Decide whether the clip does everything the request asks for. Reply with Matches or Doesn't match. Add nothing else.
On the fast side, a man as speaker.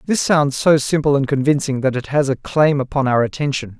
Matches